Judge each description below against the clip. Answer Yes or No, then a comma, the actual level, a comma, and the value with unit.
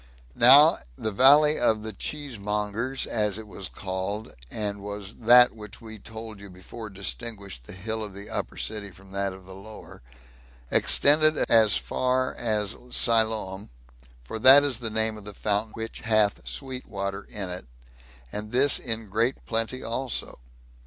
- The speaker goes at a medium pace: Yes, average, 160 wpm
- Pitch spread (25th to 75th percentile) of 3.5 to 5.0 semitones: No, average, 2.8 semitones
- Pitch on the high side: No, low, 110 Hz